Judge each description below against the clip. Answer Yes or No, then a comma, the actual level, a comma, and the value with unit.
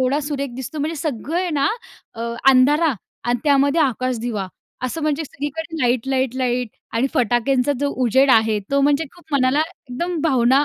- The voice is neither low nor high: No, very high, 275 Hz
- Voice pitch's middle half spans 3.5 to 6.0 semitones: No, average, 3.1 semitones